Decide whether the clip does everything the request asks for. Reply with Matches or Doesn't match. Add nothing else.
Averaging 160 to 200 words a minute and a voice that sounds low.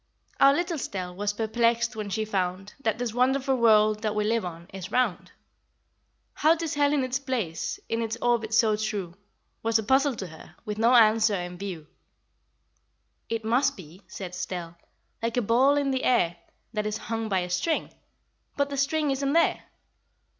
Doesn't match